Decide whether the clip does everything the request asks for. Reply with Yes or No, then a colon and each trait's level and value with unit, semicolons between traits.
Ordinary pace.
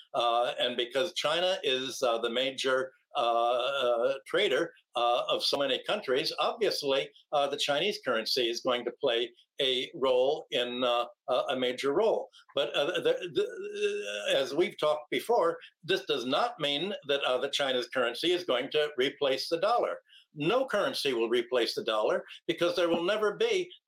Yes: average, 170 wpm